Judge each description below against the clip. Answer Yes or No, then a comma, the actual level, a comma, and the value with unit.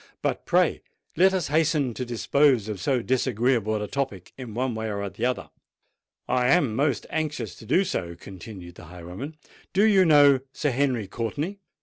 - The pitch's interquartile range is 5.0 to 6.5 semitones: Yes, average, 5.3 semitones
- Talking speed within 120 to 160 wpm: No, average, 175 wpm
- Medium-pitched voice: No, low, 125 Hz